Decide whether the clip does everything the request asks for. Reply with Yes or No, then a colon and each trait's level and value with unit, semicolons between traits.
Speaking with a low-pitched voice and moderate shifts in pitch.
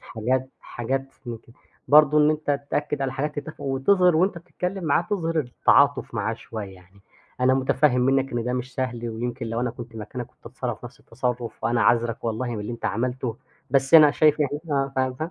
Yes: low, 130 Hz; average, 3.7 semitones